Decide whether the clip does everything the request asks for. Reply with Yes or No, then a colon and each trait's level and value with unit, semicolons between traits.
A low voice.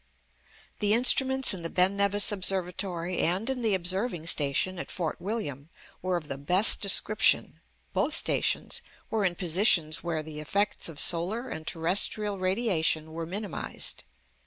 No: medium, 185 Hz